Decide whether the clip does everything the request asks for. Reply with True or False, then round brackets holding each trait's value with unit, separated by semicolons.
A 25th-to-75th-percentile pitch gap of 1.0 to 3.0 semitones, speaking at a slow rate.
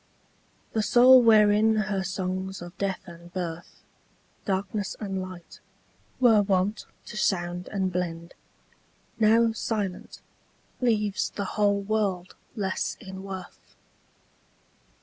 True (2.5 semitones; 110 wpm)